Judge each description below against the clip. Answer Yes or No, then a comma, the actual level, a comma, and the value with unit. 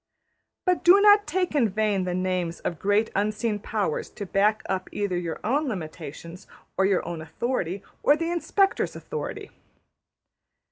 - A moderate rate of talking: Yes, average, 155 wpm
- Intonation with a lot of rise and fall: Yes, wide, 6.9 semitones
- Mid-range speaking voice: No, high, 205 Hz